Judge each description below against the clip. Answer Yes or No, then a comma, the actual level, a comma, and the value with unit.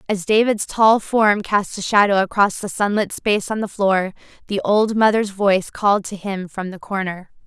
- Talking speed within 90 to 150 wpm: No, average, 195 wpm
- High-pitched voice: Yes, high, 200 Hz